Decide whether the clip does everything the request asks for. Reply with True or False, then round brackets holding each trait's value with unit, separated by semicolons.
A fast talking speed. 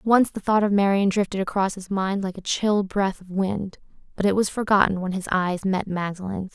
True (220 wpm)